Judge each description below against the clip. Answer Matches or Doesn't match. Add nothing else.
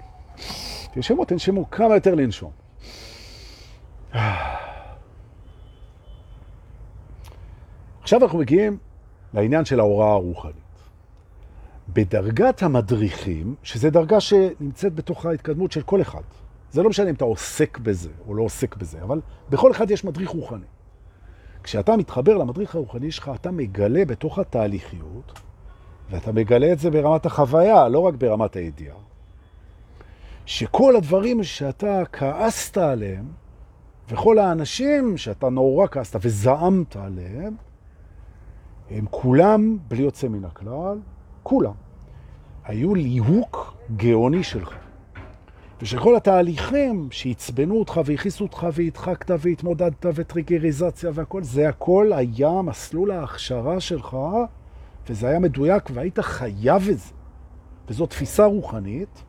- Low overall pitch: Matches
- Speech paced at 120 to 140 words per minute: Doesn't match